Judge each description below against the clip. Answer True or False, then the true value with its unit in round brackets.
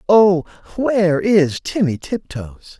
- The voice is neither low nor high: True (180 Hz)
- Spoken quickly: False (105 wpm)